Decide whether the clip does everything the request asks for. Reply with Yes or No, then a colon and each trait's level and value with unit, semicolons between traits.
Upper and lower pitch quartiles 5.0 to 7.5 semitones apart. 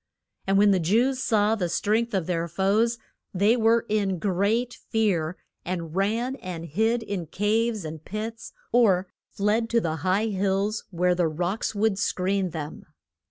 No: average, 3.8 semitones